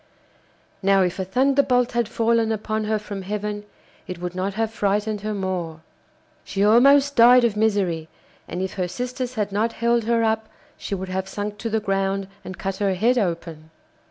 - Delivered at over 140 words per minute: Yes, average, 185 wpm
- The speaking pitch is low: No, high, 210 Hz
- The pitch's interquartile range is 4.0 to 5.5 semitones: No, average, 3.2 semitones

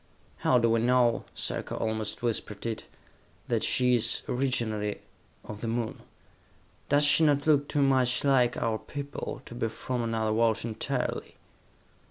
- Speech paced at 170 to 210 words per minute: No, average, 150 wpm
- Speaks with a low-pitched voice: Yes, low, 120 Hz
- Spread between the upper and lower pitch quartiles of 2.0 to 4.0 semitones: Yes, average, 2.7 semitones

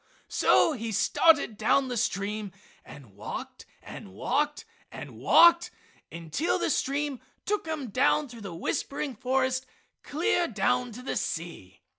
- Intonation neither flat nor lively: No, wide, 6.7 semitones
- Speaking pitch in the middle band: No, very high, 250 Hz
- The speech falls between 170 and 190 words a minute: No, slow, 135 wpm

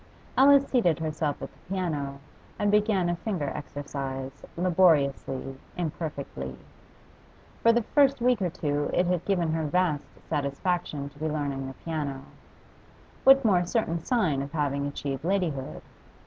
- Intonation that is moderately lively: Yes, average, 4.9 semitones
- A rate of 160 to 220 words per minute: No, average, 140 wpm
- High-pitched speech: No, medium, 160 Hz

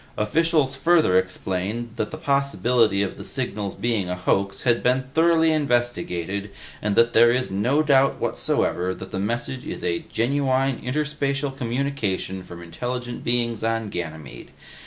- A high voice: No, low, 120 Hz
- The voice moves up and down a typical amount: No, wide, 5.7 semitones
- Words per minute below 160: Yes, average, 145 wpm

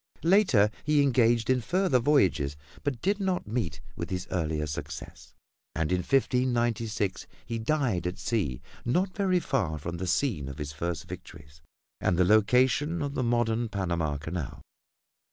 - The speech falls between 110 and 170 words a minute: Yes, average, 155 wpm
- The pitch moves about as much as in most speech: No, wide, 7.9 semitones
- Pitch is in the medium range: No, low, 110 Hz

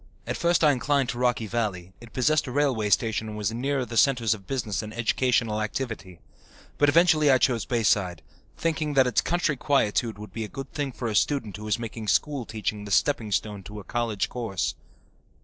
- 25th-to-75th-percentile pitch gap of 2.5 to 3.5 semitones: No, average, 4.3 semitones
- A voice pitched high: No, low, 115 Hz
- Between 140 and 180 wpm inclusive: No, average, 200 wpm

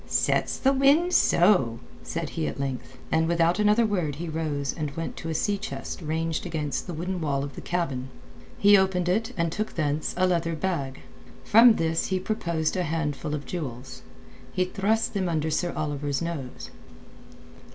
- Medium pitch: Yes, medium, 165 Hz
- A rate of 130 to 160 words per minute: No, average, 175 wpm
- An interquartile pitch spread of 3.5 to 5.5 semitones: Yes, average, 4.2 semitones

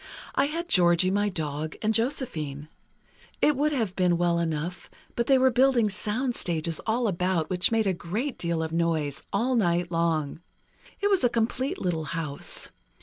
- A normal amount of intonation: No, wide, 6.3 semitones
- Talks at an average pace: Yes, average, 165 wpm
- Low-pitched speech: No, medium, 185 Hz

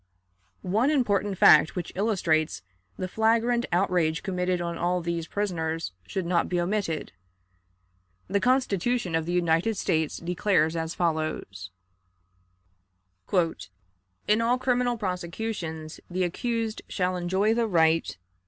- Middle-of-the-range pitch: Yes, medium, 180 Hz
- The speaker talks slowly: Yes, slow, 115 wpm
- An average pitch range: Yes, average, 4.6 semitones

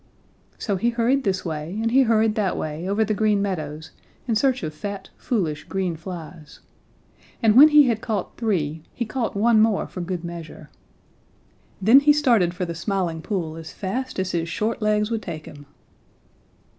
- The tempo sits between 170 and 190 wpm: Yes, average, 180 wpm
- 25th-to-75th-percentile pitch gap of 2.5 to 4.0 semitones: No, average, 5.0 semitones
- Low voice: No, high, 200 Hz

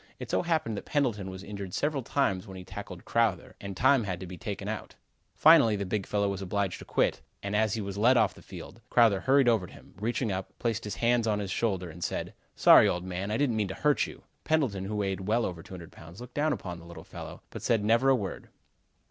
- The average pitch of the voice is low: Yes, low, 105 Hz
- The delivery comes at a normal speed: No, fast, 245 wpm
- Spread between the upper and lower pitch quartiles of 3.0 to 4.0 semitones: Yes, average, 3.7 semitones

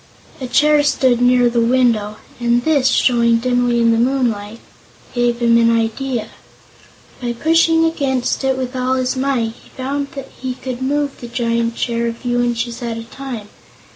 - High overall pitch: Yes, high, 245 Hz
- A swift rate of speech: No, average, 170 wpm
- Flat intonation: Yes, narrow, 2.1 semitones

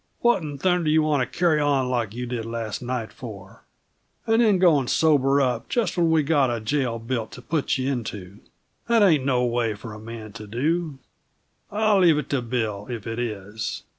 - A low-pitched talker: Yes, low, 130 Hz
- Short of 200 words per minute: No, fast, 205 wpm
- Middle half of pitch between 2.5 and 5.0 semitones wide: No, wide, 5.4 semitones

